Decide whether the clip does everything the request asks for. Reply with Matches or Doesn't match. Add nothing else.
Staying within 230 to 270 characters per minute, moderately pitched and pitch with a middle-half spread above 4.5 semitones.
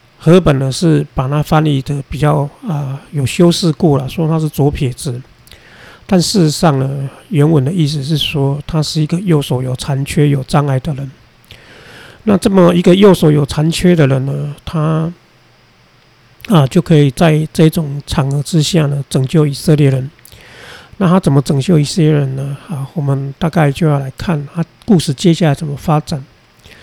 Doesn't match